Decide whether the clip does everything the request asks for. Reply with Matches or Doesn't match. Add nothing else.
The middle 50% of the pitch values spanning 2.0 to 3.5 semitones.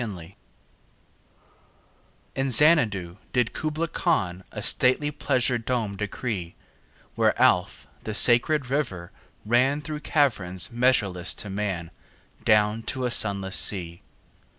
Doesn't match